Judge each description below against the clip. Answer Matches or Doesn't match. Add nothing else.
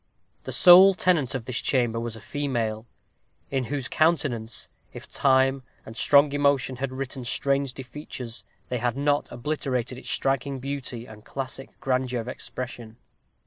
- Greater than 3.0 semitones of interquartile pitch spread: Doesn't match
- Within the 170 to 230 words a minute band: Doesn't match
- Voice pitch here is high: Doesn't match